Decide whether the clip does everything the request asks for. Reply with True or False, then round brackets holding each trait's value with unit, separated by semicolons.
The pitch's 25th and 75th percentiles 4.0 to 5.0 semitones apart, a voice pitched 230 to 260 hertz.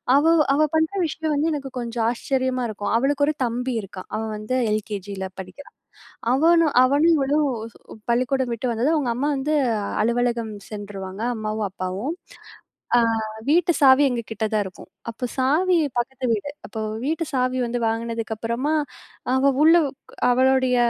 True (4.5 semitones; 255 Hz)